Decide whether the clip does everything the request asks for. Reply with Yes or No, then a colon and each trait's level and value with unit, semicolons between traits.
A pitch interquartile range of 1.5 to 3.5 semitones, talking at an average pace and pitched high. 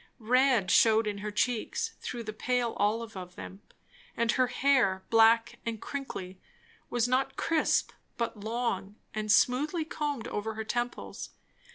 Yes: average, 2.9 semitones; average, 145 wpm; high, 230 Hz